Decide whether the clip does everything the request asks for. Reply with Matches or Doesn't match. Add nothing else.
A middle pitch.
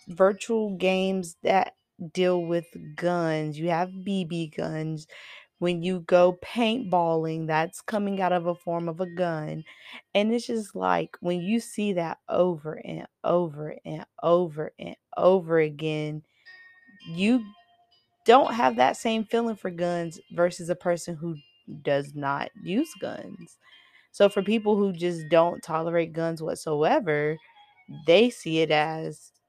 Matches